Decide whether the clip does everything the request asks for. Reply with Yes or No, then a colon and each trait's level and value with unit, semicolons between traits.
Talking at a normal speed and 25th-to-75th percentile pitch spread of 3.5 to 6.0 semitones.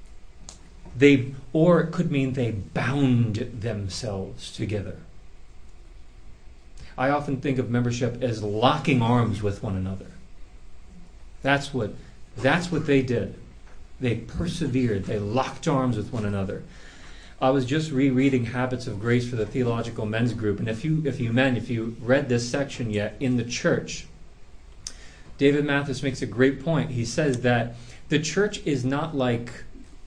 Yes: average, 150 wpm; average, 4.5 semitones